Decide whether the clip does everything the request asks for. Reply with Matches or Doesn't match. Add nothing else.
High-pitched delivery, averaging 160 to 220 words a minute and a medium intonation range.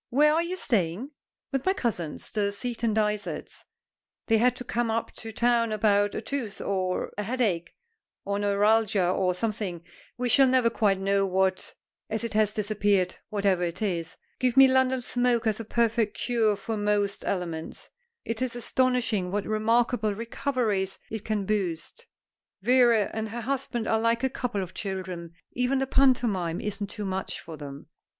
Matches